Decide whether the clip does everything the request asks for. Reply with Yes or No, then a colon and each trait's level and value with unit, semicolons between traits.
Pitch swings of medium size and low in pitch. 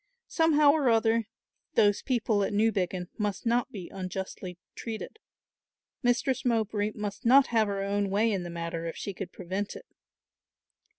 No: average, 3.5 semitones; high, 210 Hz